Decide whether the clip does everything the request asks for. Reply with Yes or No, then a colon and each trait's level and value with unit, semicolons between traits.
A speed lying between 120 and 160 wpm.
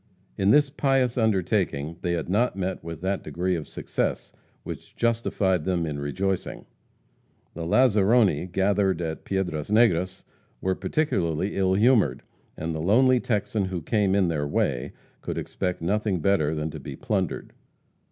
Yes: average, 150 wpm